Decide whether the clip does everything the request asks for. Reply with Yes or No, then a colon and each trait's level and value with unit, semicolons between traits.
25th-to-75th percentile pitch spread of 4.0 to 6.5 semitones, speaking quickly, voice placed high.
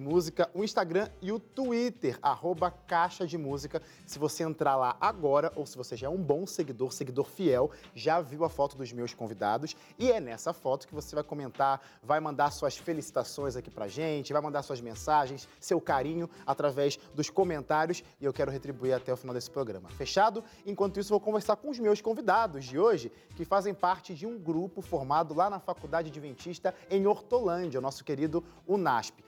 No: average, 5.1 semitones; fast, 190 wpm; medium, 160 Hz